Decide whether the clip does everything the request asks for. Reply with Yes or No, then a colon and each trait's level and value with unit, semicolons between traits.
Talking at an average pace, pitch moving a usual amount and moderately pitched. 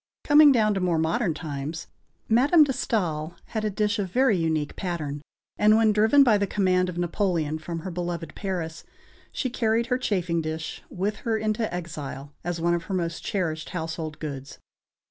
Yes: average, 180 wpm; average, 4.9 semitones; medium, 180 Hz